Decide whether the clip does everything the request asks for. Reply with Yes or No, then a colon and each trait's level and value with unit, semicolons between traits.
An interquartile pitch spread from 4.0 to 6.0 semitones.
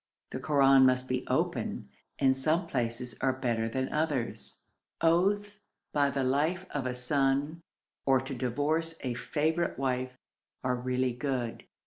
No: average, 3.2 semitones